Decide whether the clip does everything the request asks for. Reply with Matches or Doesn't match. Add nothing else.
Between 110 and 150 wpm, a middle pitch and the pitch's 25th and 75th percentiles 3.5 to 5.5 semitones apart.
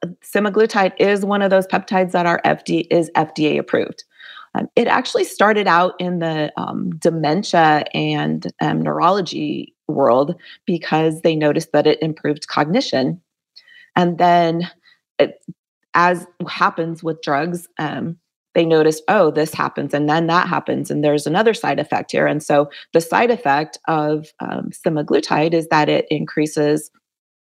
Doesn't match